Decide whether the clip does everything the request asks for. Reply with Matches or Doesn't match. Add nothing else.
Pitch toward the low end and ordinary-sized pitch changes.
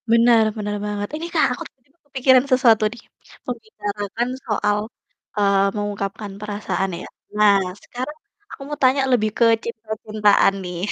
Doesn't match